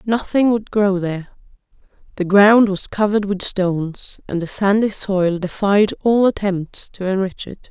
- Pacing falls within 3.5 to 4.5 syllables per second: Yes, 4.3 syllables/s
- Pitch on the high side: Yes, high, 195 Hz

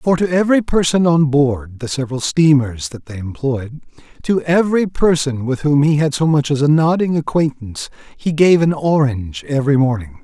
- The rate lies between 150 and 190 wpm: Yes, average, 175 wpm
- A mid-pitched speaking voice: Yes, medium, 145 Hz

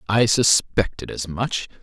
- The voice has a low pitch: Yes, low, 105 Hz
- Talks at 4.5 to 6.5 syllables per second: No, 3.9 syllables/s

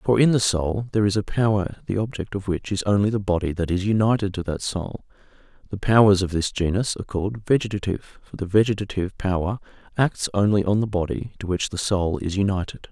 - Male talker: Yes, male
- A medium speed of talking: No, fast, 210 wpm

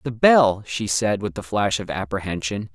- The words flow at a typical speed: Yes, average, 195 wpm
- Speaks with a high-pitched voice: No, low, 105 Hz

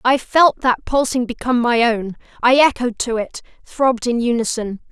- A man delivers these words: No, female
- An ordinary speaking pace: Yes, average, 170 wpm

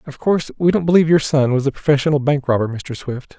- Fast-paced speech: Yes, fast, 250 wpm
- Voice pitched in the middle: Yes, medium, 145 Hz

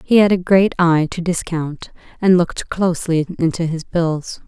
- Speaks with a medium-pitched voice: Yes, medium, 170 Hz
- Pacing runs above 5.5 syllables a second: No, 4.7 syllables/s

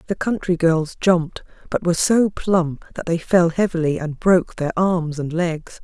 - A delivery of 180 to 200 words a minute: Yes, average, 185 wpm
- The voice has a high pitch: No, medium, 170 Hz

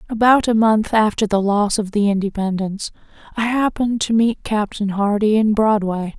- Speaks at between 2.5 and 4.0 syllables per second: No, 5.1 syllables/s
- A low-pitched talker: No, high, 215 Hz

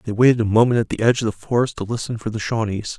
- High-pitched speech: No, low, 115 Hz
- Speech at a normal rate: No, fast, 300 wpm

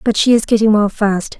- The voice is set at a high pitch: Yes, high, 215 Hz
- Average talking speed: No, fast, 260 wpm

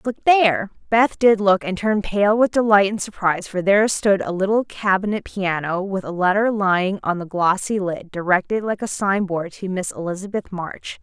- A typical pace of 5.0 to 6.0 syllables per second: Yes, 5.1 syllables/s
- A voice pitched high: Yes, high, 195 Hz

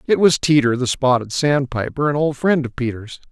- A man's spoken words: Yes, male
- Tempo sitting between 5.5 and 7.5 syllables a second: No, 5.2 syllables/s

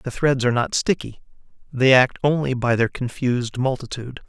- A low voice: Yes, low, 130 Hz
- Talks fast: No, average, 170 wpm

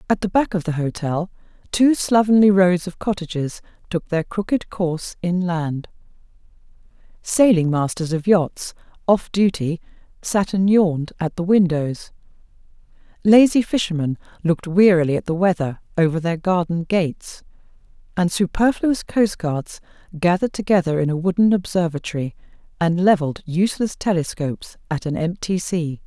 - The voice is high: No, medium, 180 Hz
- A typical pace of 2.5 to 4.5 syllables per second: No, 5.0 syllables/s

